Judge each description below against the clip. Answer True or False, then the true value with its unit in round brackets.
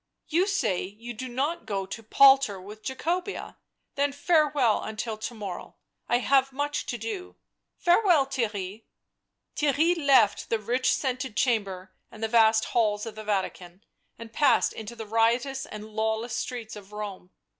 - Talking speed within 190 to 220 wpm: False (155 wpm)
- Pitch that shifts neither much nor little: True (4.5 semitones)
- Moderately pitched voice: False (230 Hz)